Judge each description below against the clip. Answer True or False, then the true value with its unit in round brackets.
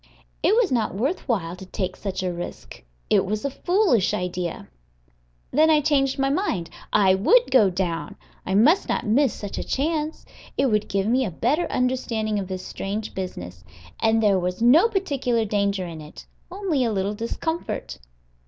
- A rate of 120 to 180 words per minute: True (175 wpm)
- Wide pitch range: True (6.8 semitones)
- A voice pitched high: True (220 Hz)